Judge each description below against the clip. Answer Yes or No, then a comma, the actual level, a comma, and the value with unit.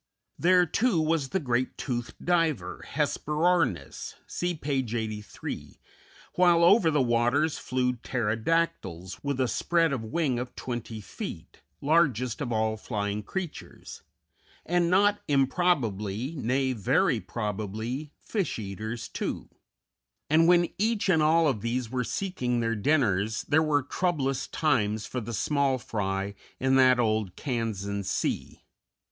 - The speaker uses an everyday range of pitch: No, wide, 6.6 semitones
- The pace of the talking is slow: Yes, slow, 130 wpm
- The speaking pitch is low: Yes, low, 130 Hz